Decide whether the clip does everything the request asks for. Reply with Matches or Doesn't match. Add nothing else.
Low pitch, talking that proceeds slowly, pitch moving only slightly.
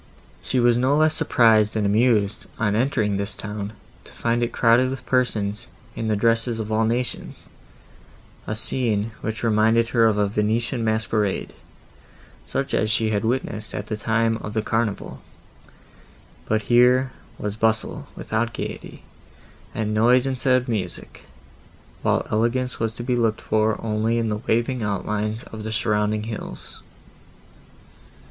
Doesn't match